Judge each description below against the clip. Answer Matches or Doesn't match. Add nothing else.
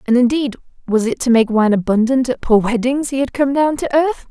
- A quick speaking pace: Matches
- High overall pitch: Matches